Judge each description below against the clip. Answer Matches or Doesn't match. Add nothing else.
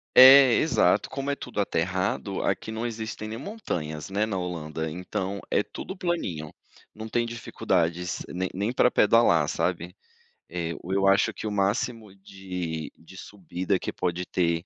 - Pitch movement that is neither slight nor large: Matches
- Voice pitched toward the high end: Doesn't match